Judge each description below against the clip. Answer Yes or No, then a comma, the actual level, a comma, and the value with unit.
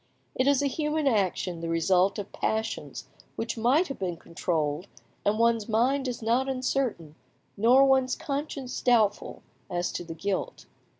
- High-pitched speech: Yes, high, 225 Hz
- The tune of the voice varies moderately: No, wide, 6.1 semitones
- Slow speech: No, average, 155 wpm